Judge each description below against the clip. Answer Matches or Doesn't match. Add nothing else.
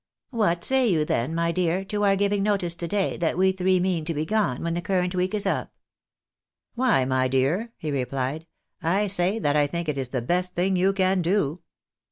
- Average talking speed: Doesn't match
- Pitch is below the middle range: Doesn't match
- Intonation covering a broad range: Doesn't match